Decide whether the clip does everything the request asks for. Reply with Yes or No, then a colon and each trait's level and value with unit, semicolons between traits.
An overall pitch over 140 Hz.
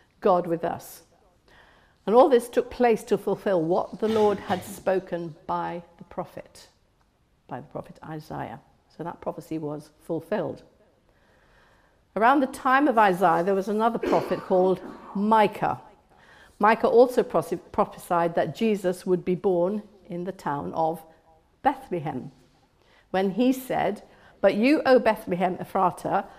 Yes: medium, 185 Hz